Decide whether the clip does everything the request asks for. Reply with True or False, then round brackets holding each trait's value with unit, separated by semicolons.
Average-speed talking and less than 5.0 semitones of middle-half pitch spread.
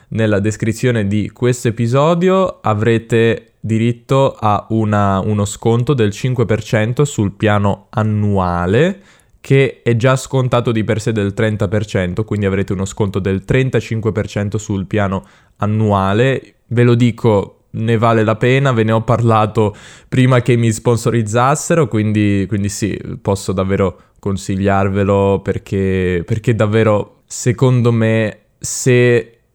True (125 wpm; 2.9 semitones)